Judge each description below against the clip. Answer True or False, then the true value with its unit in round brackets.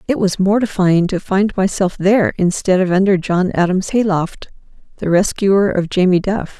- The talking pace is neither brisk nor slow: True (165 wpm)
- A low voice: False (190 Hz)